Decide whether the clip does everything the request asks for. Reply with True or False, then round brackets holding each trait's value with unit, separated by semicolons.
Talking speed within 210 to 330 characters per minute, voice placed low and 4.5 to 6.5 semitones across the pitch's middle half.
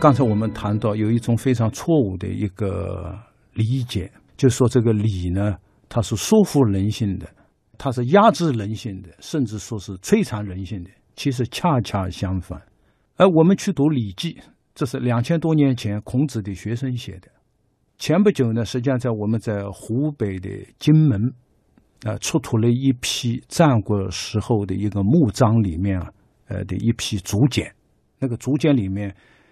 True (250 characters per minute; 115 Hz; 5.0 semitones)